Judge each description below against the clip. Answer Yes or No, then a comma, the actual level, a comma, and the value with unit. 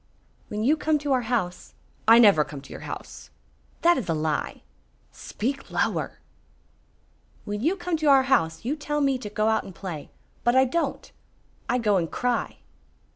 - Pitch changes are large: Yes, wide, 6.0 semitones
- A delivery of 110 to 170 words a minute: No, average, 180 wpm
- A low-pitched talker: No, high, 240 Hz